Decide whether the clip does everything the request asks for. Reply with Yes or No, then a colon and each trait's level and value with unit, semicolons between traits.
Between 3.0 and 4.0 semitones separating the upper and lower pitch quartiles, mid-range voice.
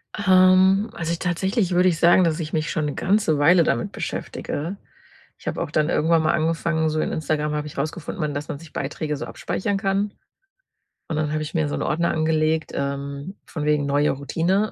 Yes: average, 3.4 semitones; medium, 160 Hz